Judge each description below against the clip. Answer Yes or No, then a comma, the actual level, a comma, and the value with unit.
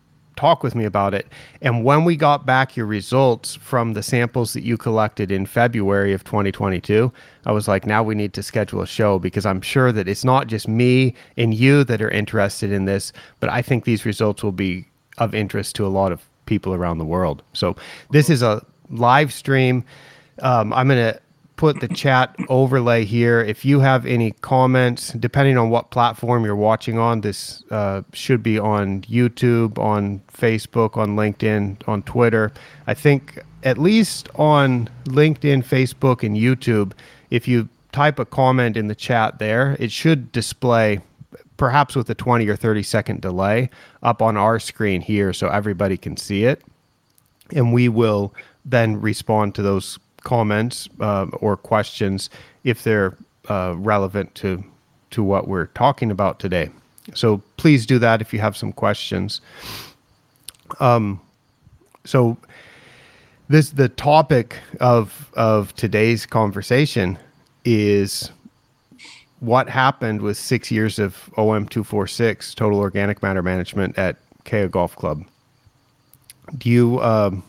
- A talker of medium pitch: No, low, 115 Hz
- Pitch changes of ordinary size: Yes, average, 3.7 semitones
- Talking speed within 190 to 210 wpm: No, average, 155 wpm